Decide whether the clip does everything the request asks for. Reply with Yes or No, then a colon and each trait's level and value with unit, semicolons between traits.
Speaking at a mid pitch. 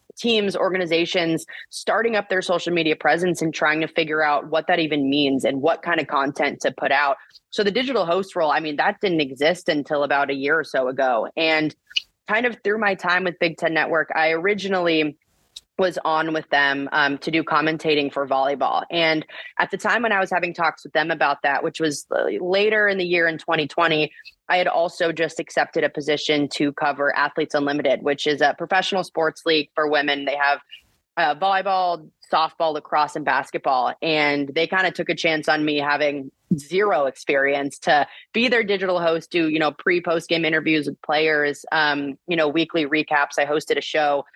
Yes: medium, 160 Hz